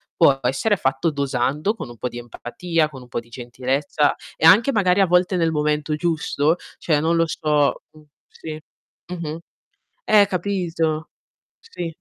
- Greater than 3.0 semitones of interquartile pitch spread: Yes, average, 4.0 semitones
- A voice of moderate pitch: Yes, medium, 155 Hz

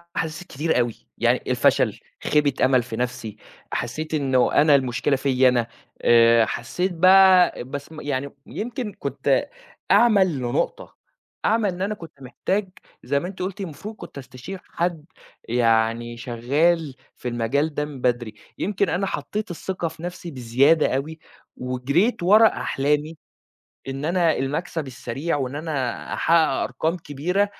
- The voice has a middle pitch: Yes, medium, 150 Hz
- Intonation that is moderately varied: No, wide, 5.8 semitones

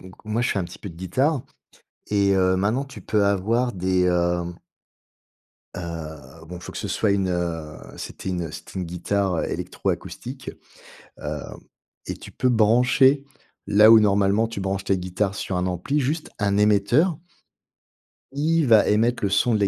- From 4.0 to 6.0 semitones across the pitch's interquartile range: Yes, average, 4.4 semitones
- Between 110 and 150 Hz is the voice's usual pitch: No, low, 100 Hz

